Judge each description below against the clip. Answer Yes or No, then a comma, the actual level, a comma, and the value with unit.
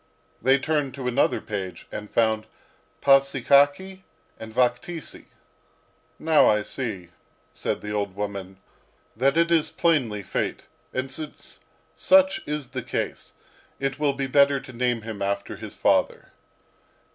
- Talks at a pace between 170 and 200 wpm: No, slow, 135 wpm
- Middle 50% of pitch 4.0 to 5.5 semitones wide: Yes, average, 4.9 semitones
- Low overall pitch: Yes, low, 130 Hz